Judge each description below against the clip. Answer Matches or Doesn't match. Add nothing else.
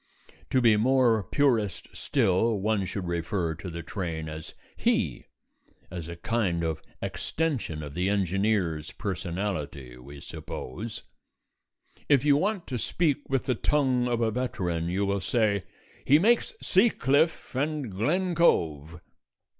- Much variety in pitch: Matches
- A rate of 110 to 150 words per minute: Matches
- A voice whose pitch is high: Doesn't match